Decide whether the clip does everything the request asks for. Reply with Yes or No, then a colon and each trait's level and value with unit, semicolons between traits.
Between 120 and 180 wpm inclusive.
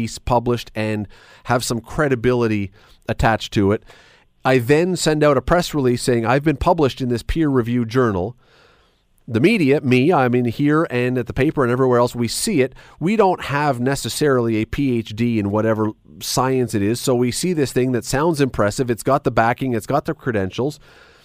No: average, 190 wpm